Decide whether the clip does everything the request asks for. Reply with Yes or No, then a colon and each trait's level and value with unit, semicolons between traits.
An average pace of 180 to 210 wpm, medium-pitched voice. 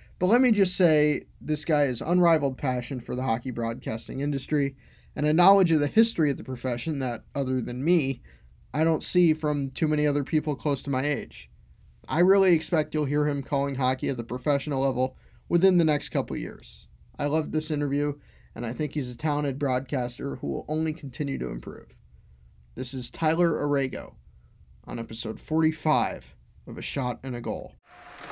Yes: average, 185 wpm; medium, 145 Hz